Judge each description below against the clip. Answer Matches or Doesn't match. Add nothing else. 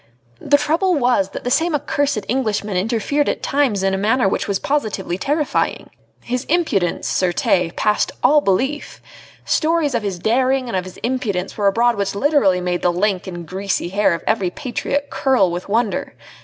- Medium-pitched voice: Doesn't match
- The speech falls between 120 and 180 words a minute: Matches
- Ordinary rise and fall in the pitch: Doesn't match